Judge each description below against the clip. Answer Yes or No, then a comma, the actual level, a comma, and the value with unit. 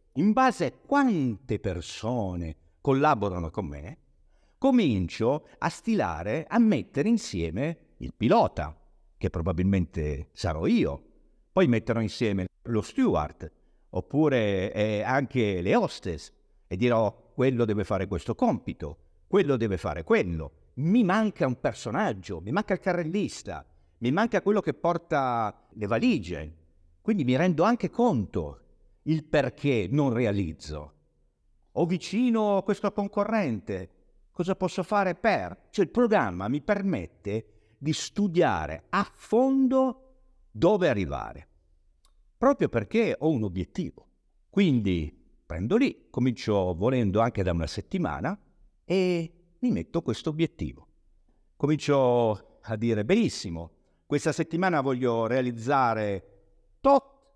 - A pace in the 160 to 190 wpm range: No, average, 120 wpm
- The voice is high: No, low, 125 Hz